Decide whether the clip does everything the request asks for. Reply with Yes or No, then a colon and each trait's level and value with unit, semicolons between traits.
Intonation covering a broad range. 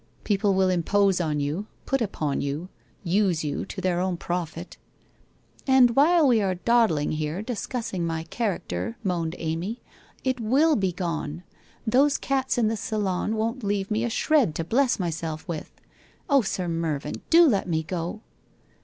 Yes: wide, 5.7 semitones